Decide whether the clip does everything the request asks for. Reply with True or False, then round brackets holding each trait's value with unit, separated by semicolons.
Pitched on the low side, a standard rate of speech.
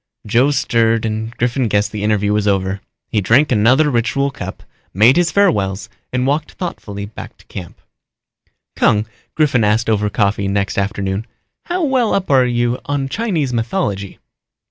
True (115 Hz; 155 wpm)